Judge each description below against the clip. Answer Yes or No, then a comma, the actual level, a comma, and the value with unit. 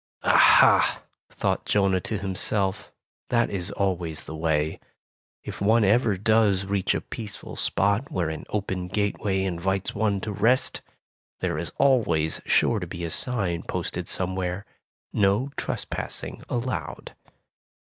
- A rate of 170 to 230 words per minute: No, slow, 135 wpm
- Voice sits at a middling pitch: No, very low, 95 Hz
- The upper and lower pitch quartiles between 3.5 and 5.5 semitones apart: No, average, 3.1 semitones